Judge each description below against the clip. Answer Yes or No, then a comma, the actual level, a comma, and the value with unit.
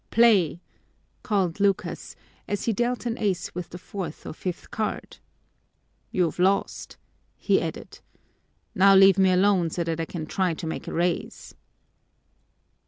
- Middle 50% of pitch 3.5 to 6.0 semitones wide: No, average, 2.8 semitones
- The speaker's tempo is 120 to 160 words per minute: Yes, average, 145 wpm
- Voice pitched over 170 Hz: Yes, medium, 185 Hz